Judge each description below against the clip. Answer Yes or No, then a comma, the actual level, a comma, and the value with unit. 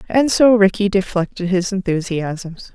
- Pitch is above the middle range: Yes, high, 195 Hz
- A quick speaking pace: No, slow, 130 wpm